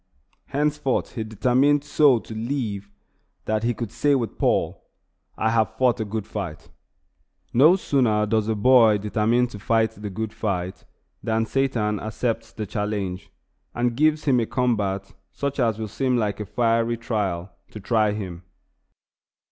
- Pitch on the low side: Yes, low, 110 Hz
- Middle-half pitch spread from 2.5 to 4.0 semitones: Yes, average, 3.0 semitones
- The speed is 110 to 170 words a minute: Yes, average, 155 wpm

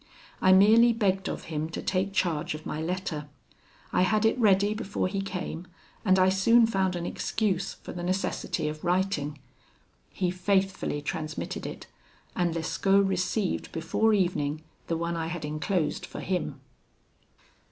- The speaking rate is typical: Yes, average, 150 wpm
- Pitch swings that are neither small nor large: Yes, average, 3.2 semitones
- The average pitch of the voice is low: No, medium, 185 Hz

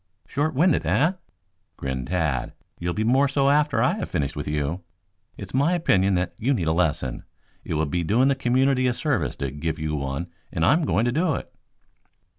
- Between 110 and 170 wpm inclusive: No, average, 200 wpm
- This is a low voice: Yes, low, 100 Hz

